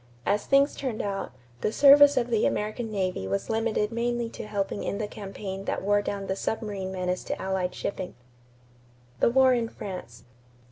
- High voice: Yes, high, 210 Hz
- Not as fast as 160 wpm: No, average, 175 wpm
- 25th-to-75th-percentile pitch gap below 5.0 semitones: Yes, average, 3.5 semitones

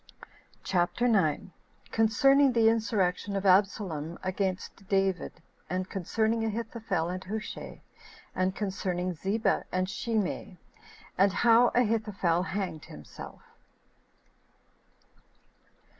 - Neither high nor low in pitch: No, high, 195 Hz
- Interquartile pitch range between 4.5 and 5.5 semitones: No, average, 3.3 semitones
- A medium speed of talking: No, slow, 90 wpm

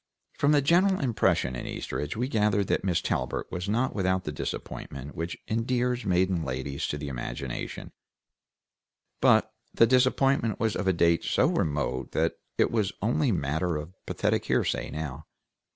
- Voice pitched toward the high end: No, very low, 95 Hz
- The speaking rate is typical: Yes, average, 155 wpm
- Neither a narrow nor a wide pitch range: No, wide, 7.8 semitones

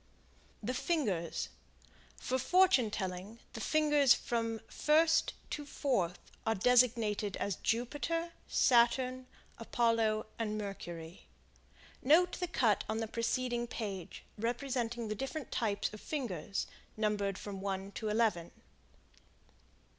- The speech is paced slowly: Yes, slow, 110 wpm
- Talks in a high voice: Yes, high, 230 Hz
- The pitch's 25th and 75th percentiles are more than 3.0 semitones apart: Yes, average, 4.0 semitones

